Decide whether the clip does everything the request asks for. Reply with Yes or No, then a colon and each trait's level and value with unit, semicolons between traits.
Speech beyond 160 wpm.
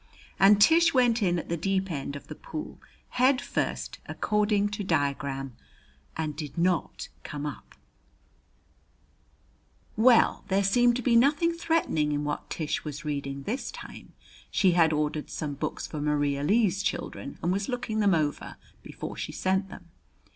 No: average, 155 wpm